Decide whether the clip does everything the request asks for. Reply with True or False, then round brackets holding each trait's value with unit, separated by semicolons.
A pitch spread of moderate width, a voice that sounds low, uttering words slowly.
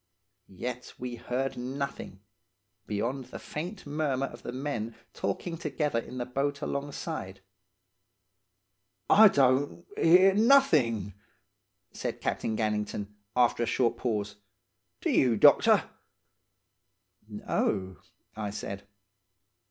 True (4.8 semitones; 125 Hz; 105 wpm)